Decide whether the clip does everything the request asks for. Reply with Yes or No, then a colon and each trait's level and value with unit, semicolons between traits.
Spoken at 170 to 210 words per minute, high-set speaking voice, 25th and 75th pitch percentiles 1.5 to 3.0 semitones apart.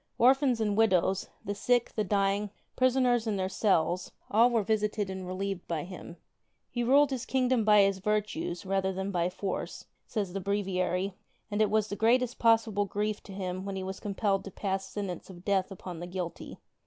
Yes: average, 190 wpm; high, 200 Hz; average, 2.7 semitones